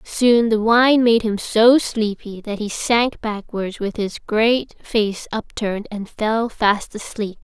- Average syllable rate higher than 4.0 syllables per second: No, 3.5 syllables/s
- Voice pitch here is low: No, high, 220 Hz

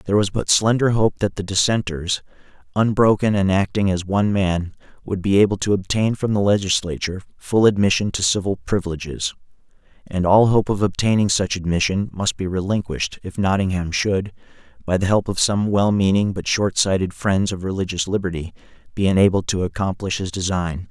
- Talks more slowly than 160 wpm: No, average, 165 wpm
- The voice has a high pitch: No, very low, 95 Hz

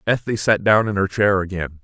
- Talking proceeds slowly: No, fast, 230 wpm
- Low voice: Yes, low, 100 Hz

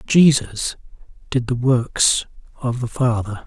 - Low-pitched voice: Yes, low, 125 Hz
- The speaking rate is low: Yes, slow, 120 wpm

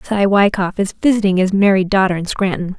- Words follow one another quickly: No, average, 195 wpm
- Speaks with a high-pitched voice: Yes, high, 195 Hz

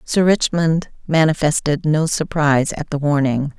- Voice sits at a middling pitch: Yes, medium, 155 Hz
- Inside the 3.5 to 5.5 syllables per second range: Yes, 4.5 syllables/s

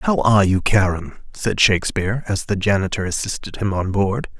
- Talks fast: No, average, 180 wpm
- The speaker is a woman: No, male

